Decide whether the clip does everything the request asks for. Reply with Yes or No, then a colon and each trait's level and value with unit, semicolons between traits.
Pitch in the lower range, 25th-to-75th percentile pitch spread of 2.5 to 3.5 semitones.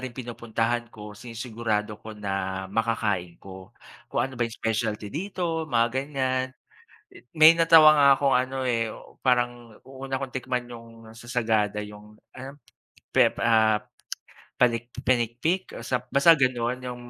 Yes: low, 120 Hz; average, 3.0 semitones